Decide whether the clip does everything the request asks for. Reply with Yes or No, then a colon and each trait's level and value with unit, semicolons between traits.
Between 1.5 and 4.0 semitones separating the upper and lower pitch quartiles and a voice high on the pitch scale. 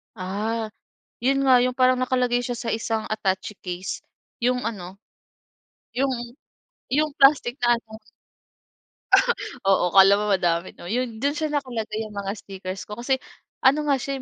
No: average, 4.4 semitones; high, 235 Hz